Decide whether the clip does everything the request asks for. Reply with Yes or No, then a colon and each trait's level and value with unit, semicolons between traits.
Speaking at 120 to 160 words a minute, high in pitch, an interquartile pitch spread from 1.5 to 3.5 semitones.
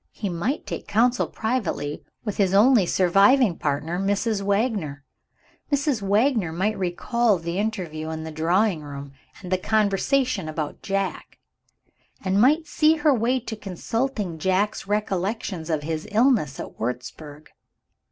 No: slow, 135 wpm; high, 195 Hz; wide, 5.6 semitones